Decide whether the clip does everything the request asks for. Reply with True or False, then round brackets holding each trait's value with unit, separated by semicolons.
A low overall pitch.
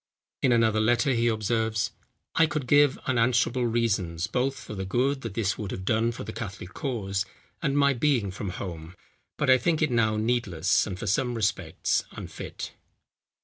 True (115 Hz)